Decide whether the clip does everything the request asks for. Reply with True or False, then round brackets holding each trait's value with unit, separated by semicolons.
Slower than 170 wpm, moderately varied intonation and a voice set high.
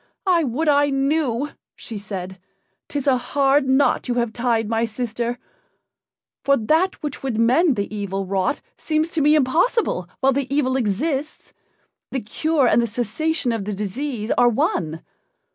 True (160 wpm; 4.9 semitones; 255 Hz)